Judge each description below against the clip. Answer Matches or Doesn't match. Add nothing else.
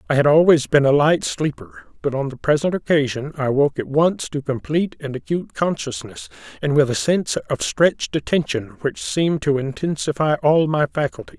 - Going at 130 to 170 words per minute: Doesn't match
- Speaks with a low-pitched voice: Doesn't match